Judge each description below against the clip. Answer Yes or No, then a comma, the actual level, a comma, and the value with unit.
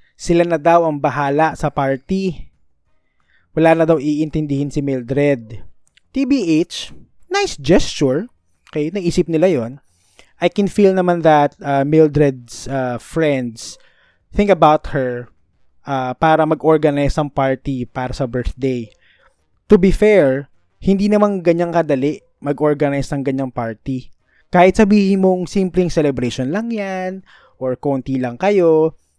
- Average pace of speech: Yes, average, 125 wpm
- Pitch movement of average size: Yes, average, 5.0 semitones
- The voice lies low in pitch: No, medium, 150 Hz